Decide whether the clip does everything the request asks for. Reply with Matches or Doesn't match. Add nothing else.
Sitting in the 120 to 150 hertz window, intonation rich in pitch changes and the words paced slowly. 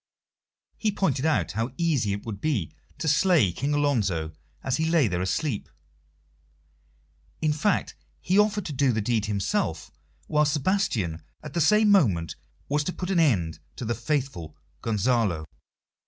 Doesn't match